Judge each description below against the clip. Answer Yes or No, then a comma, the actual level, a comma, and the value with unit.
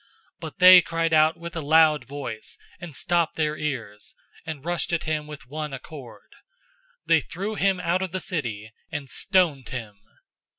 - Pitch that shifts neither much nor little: Yes, average, 3.9 semitones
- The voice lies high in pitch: No, medium, 155 Hz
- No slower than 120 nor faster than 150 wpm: No, average, 175 wpm